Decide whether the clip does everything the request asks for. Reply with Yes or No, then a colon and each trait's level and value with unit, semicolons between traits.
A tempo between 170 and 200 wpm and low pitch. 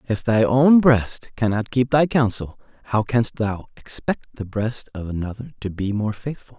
Yes: average, 180 wpm; low, 115 Hz